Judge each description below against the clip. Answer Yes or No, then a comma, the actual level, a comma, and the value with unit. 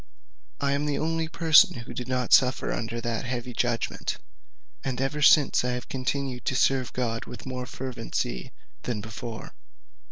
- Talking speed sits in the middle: Yes, average, 160 wpm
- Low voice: Yes, low, 125 Hz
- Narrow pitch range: Yes, narrow, 2.2 semitones